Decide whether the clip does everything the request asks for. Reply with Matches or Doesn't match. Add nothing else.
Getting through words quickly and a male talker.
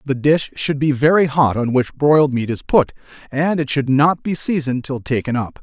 Matches